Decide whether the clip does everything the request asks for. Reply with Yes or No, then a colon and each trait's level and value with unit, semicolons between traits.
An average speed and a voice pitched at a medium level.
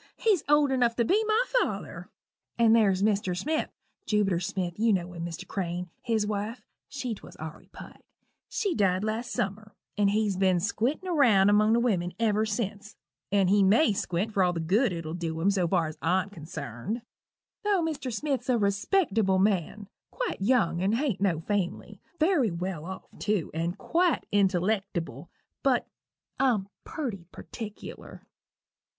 No: average, 160 wpm; high, 205 Hz